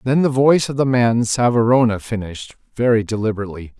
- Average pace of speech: Yes, average, 160 wpm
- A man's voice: Yes, male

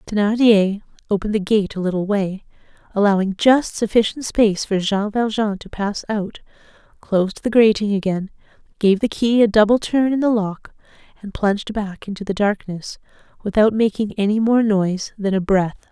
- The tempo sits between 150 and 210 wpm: Yes, average, 165 wpm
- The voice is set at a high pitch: Yes, high, 205 Hz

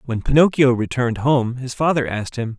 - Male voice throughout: Yes, male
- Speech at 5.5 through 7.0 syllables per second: Yes, 5.7 syllables/s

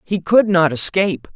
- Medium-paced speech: Yes, average, 175 wpm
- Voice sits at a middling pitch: Yes, medium, 180 Hz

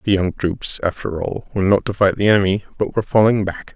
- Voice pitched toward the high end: No, low, 100 Hz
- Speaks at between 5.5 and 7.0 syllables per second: Yes, 6.1 syllables/s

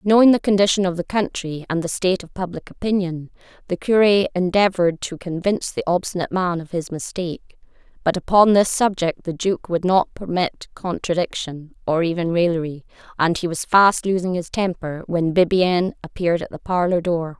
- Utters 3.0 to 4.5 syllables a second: No, 5.3 syllables/s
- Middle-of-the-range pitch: Yes, medium, 180 Hz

